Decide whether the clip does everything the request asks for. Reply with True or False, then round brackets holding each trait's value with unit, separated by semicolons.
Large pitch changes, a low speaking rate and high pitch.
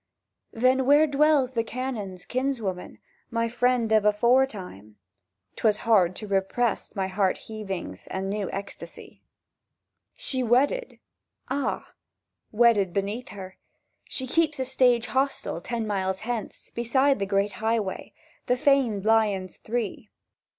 False (4.4 semitones; 115 wpm; 225 Hz)